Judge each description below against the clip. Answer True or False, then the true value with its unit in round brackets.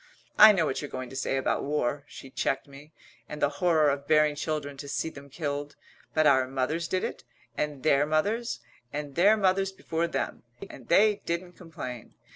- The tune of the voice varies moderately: True (3.3 semitones)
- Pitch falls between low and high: True (150 Hz)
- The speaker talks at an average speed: True (190 wpm)